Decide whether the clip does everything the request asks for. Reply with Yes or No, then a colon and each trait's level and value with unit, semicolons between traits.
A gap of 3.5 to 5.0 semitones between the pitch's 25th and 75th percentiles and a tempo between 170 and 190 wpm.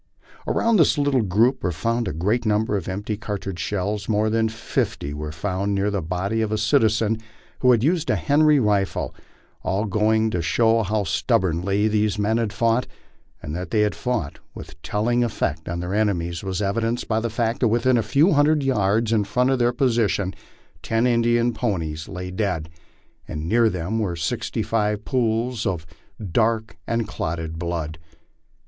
Yes: average, 3.9 semitones; average, 180 wpm